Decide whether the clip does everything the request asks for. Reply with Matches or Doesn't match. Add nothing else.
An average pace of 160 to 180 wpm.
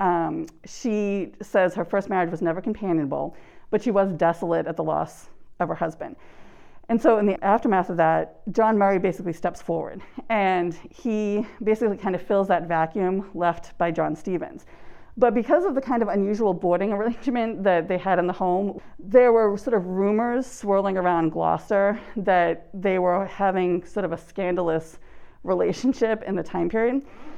Matches